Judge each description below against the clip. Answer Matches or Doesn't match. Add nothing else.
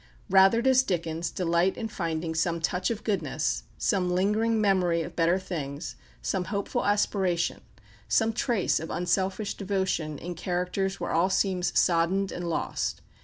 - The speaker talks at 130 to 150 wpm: Matches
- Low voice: Doesn't match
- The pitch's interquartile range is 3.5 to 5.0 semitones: Doesn't match